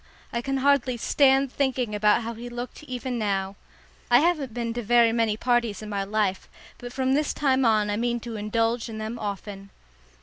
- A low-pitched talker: No, high, 235 Hz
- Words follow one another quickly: No, average, 195 wpm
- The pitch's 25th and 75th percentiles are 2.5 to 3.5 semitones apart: Yes, average, 3.2 semitones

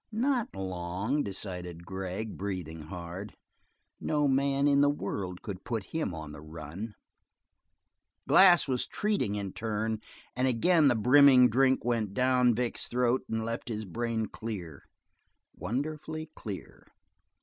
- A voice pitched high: No, low, 110 Hz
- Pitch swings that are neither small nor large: No, wide, 6.0 semitones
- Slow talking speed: Yes, slow, 130 wpm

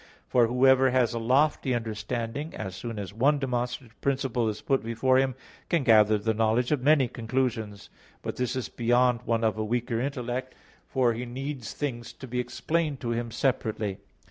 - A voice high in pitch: No, low, 125 Hz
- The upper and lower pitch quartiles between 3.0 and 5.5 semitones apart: No, narrow, 2.5 semitones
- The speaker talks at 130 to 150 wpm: No, average, 175 wpm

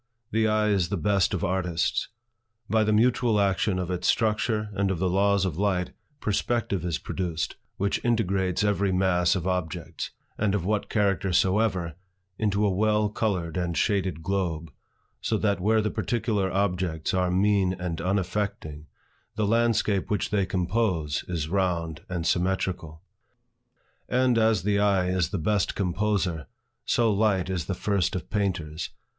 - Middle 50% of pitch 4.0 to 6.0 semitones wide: No, average, 2.9 semitones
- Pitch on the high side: No, very low, 95 Hz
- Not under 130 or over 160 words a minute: Yes, average, 150 wpm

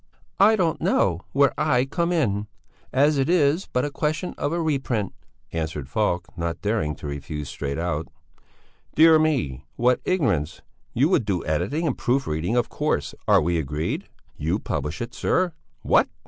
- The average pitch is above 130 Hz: No, low, 120 Hz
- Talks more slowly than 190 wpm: Yes, average, 170 wpm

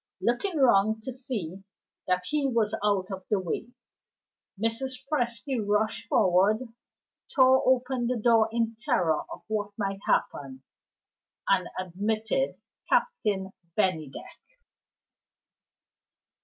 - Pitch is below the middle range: No, high, 220 Hz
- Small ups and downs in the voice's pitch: No, average, 4.3 semitones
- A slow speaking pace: Yes, slow, 105 wpm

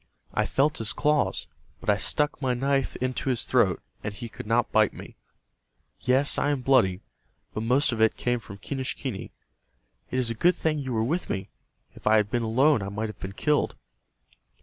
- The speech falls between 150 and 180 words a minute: No, average, 195 wpm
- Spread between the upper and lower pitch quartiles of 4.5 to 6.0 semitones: No, average, 4.0 semitones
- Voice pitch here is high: No, low, 125 Hz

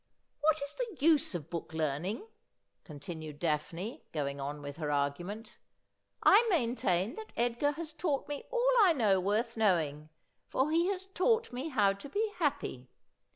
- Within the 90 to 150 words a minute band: No, average, 170 wpm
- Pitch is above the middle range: Yes, high, 225 Hz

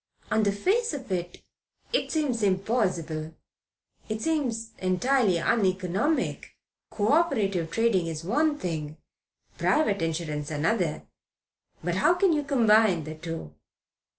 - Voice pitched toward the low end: No, high, 200 Hz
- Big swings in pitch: Yes, wide, 7.0 semitones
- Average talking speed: No, slow, 120 wpm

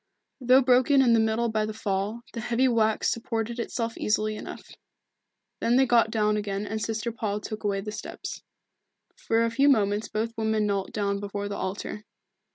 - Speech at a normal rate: Yes, average, 180 wpm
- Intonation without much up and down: Yes, narrow, 1.9 semitones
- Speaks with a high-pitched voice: Yes, high, 220 Hz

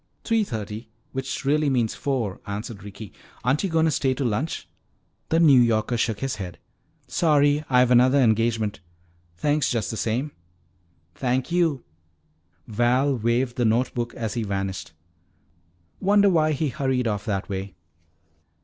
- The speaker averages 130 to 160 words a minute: Yes, average, 150 wpm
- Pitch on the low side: Yes, low, 125 Hz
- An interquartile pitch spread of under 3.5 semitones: No, average, 4.5 semitones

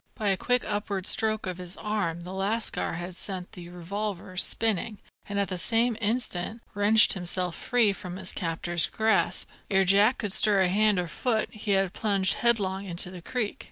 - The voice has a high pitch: Yes, high, 200 Hz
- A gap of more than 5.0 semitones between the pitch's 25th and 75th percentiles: No, average, 3.0 semitones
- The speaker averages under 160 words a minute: No, average, 180 wpm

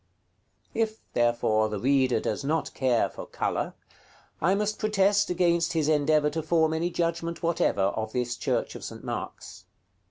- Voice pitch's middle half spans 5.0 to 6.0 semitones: Yes, wide, 5.5 semitones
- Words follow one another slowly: No, average, 155 wpm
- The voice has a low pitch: No, medium, 155 Hz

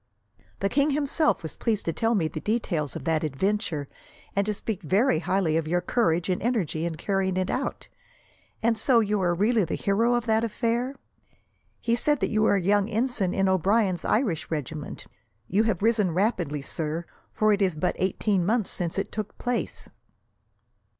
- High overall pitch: Yes, high, 200 Hz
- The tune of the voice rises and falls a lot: No, average, 4.7 semitones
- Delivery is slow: No, average, 185 wpm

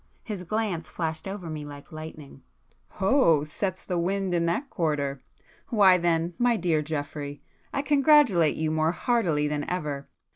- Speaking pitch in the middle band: Yes, medium, 170 Hz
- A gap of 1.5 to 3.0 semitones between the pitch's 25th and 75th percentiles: No, average, 4.4 semitones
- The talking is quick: No, average, 145 wpm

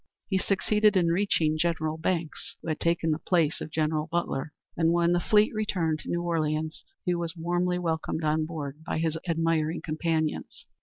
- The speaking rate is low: No, average, 175 wpm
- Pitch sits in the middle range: Yes, medium, 165 Hz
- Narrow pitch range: Yes, narrow, 1.9 semitones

